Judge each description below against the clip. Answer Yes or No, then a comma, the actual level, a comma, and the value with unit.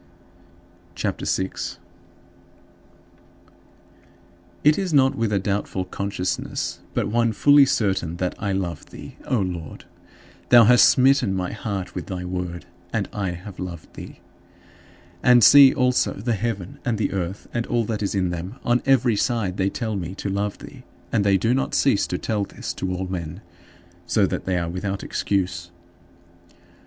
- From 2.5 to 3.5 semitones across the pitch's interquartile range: No, average, 4.2 semitones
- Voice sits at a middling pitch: No, low, 100 Hz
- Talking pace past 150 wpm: Yes, average, 160 wpm